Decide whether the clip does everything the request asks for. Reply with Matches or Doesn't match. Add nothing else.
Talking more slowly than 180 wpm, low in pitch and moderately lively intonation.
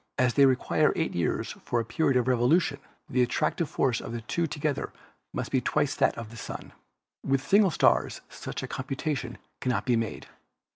Doesn't match